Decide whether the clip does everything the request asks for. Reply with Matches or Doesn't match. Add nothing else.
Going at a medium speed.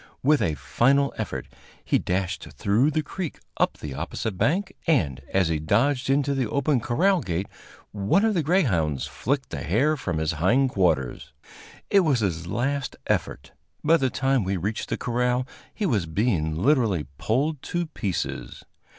Matches